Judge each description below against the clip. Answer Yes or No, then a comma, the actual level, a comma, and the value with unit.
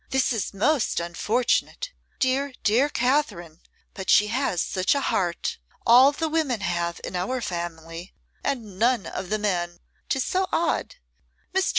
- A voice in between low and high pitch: No, high, 225 Hz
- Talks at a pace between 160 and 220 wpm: No, average, 150 wpm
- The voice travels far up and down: Yes, wide, 7.4 semitones